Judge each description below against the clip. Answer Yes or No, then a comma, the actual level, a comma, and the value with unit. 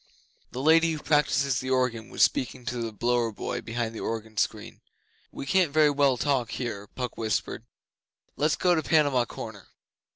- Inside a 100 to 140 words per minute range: No, average, 170 wpm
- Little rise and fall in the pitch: No, average, 4.2 semitones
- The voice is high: No, low, 130 Hz